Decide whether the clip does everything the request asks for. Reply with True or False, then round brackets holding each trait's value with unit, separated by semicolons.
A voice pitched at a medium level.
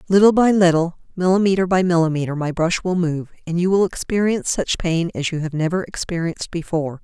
True (175 Hz)